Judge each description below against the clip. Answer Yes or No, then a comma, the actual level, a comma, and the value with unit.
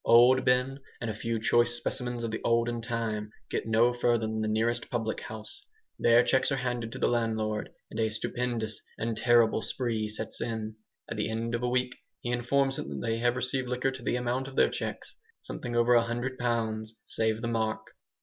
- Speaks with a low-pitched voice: Yes, low, 115 Hz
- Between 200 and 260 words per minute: Yes, fast, 205 wpm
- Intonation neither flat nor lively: No, narrow, 1.7 semitones